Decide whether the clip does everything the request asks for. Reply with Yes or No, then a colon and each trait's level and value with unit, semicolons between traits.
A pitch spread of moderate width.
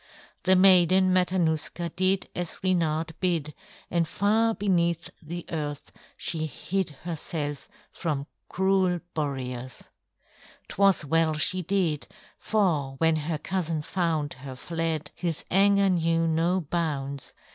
Yes: average, 3.3 semitones